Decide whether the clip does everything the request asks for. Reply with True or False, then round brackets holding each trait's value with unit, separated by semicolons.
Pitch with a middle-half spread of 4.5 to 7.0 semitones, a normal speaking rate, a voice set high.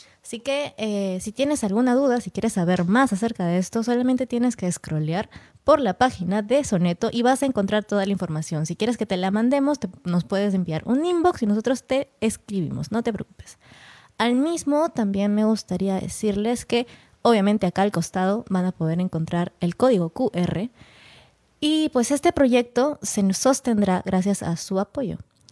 True (5.1 semitones; 180 wpm; 215 Hz)